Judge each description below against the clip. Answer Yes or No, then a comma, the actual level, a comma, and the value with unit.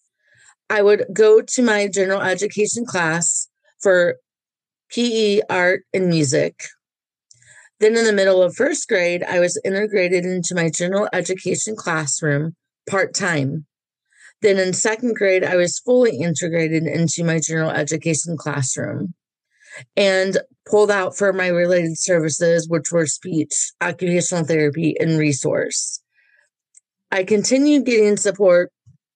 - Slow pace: Yes, slow, 125 wpm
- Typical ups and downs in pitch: Yes, average, 4.0 semitones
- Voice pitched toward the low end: No, medium, 180 Hz